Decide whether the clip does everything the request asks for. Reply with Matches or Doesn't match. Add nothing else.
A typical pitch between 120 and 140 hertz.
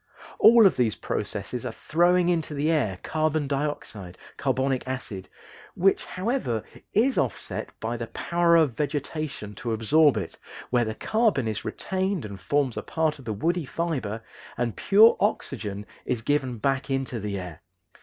Matches